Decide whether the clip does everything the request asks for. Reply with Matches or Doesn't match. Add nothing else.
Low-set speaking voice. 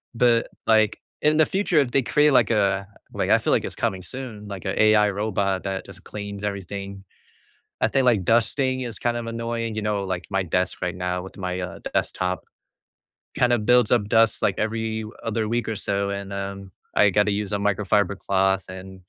Matches